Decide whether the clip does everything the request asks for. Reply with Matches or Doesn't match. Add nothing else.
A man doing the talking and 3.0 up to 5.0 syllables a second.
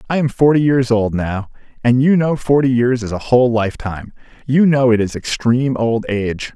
Doesn't match